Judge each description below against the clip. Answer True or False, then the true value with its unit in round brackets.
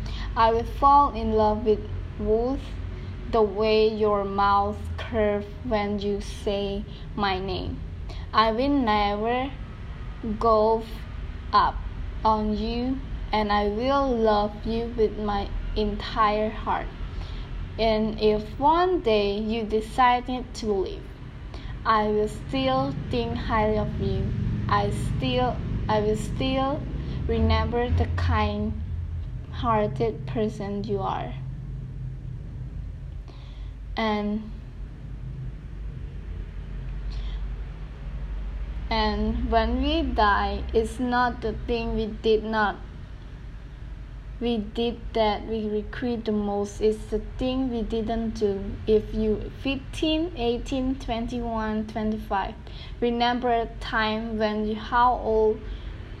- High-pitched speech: True (215 Hz)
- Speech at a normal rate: False (105 wpm)